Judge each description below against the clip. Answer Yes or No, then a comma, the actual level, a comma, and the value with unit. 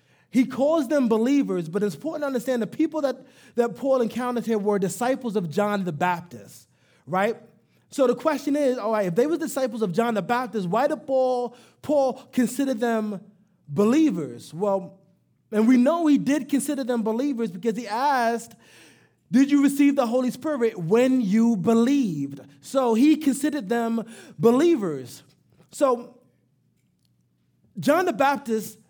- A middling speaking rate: Yes, average, 155 wpm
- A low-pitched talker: No, high, 235 Hz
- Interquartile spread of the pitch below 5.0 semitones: Yes, average, 4.6 semitones